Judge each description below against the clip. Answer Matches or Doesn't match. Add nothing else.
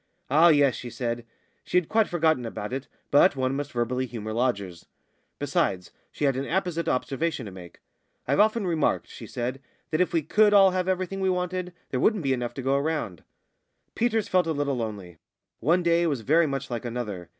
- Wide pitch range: Matches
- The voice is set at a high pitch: Doesn't match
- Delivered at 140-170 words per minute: Doesn't match